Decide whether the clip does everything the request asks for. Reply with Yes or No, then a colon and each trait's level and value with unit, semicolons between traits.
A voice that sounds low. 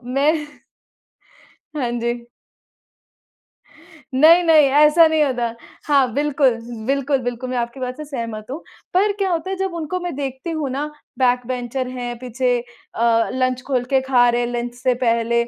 No: very high, 260 Hz